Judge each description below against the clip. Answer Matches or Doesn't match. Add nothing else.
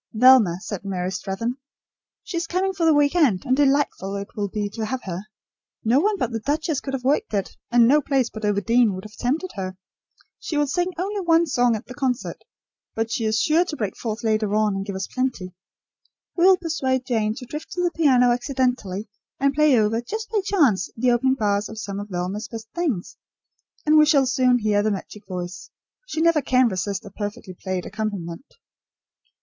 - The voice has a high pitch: Matches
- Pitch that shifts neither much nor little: Doesn't match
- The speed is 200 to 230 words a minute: Matches